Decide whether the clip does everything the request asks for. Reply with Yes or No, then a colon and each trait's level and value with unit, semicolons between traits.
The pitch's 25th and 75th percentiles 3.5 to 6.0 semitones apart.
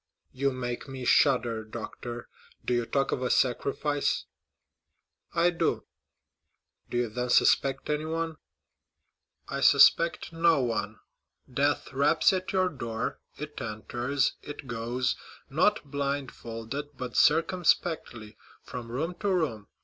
Yes: average, 4.2 semitones